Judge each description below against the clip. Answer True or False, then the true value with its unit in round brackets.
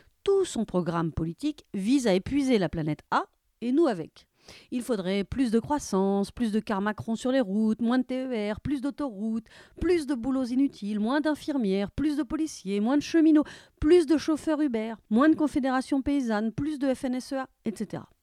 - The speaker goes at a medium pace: True (180 wpm)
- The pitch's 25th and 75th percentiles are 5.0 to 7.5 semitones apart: True (5.6 semitones)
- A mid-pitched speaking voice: False (255 Hz)